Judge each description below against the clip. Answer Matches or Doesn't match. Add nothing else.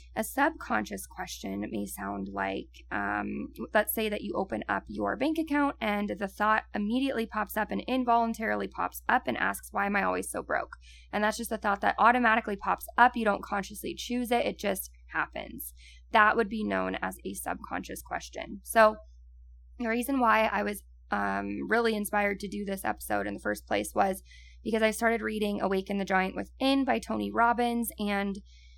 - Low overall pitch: Doesn't match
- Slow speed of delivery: Doesn't match